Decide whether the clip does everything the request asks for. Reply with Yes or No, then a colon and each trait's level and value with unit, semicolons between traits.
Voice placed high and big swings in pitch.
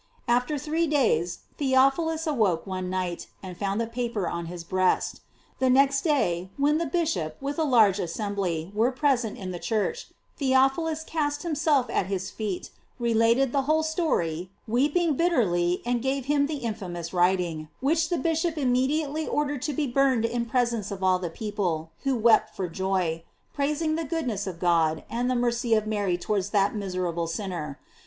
Yes: high, 235 Hz; wide, 7.4 semitones